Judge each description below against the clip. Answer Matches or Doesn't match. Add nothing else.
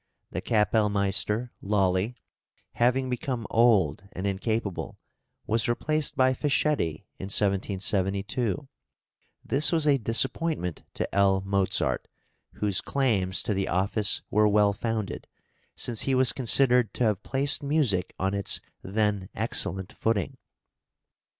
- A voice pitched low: Matches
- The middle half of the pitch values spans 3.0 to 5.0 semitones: Matches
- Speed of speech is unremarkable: Doesn't match